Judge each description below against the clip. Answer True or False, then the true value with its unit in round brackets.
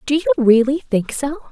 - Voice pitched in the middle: False (265 Hz)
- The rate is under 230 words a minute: True (200 wpm)